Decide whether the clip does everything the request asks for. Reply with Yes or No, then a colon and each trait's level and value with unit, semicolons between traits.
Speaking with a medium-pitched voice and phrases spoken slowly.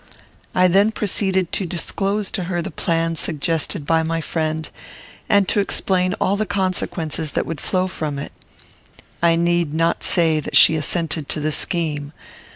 No: medium, 170 Hz; average, 165 wpm